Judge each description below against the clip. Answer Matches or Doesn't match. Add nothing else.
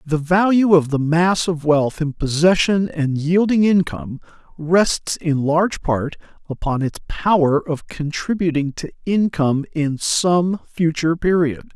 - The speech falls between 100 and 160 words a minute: Matches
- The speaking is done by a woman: Doesn't match